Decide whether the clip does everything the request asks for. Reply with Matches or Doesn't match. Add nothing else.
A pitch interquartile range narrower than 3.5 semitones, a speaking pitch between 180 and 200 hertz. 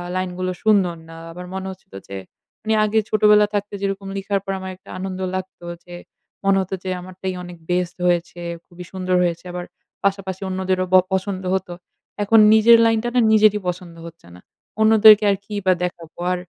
Matches